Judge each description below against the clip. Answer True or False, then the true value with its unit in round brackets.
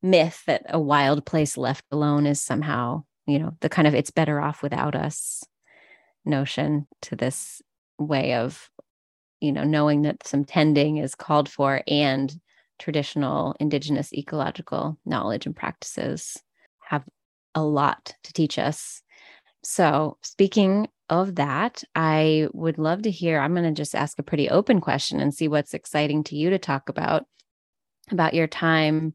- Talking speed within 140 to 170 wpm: True (155 wpm)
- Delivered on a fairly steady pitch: True (2.0 semitones)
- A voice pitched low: False (150 Hz)